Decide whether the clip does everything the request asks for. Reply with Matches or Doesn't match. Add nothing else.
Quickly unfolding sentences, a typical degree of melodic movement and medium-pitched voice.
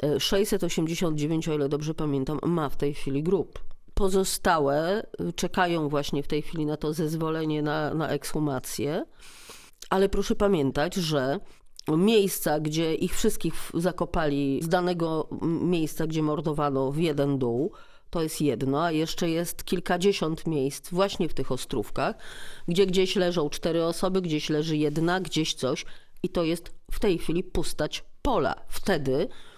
Doesn't match